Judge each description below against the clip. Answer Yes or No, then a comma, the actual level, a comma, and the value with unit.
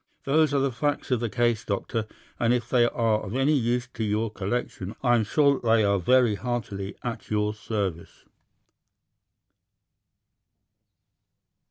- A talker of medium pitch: No, low, 115 Hz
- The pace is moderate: Yes, average, 150 wpm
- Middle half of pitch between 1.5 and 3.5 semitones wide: Yes, average, 2.9 semitones